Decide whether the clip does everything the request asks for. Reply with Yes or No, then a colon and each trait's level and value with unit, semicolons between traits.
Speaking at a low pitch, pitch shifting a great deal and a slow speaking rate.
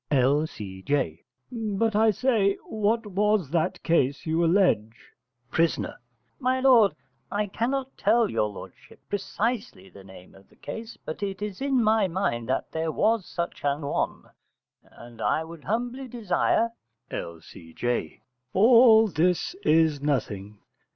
No: medium, 185 Hz; wide, 7.9 semitones; slow, 130 wpm